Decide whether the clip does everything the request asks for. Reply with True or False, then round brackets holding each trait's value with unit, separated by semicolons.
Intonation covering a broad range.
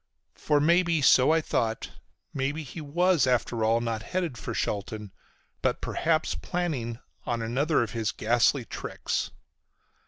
True (5.8 semitones)